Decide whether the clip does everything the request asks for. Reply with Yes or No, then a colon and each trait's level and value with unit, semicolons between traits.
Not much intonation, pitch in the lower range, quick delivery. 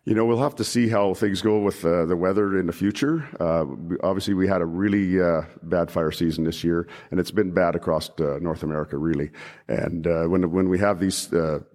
No: average, 3.1 semitones; very low, 95 Hz; fast, 230 wpm